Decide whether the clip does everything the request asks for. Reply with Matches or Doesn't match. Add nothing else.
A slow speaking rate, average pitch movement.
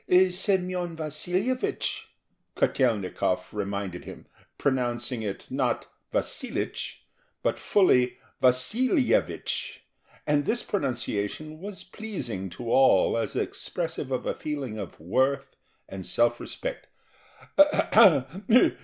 Doesn't match